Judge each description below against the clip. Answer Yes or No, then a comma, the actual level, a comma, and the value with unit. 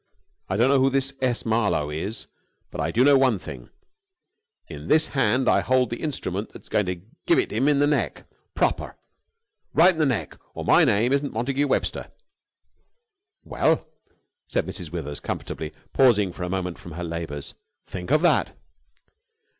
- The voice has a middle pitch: No, low, 115 Hz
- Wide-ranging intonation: Yes, wide, 7.0 semitones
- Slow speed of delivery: No, average, 170 wpm